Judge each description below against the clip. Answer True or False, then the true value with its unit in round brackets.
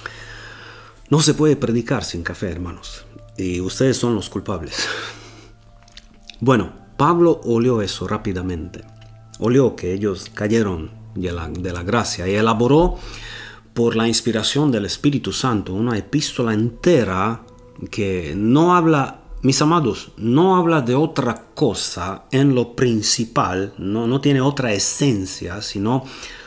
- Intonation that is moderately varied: True (4.5 semitones)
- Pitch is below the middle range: True (115 Hz)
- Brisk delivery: False (120 wpm)